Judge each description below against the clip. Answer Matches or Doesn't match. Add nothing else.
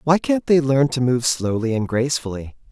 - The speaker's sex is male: Matches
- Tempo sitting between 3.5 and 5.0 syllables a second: Doesn't match